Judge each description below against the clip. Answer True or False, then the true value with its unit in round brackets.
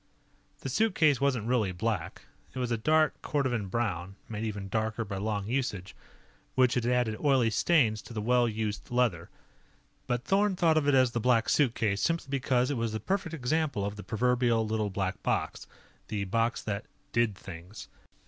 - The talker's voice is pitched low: True (115 Hz)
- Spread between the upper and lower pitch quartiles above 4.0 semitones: False (3.7 semitones)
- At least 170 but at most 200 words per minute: True (175 wpm)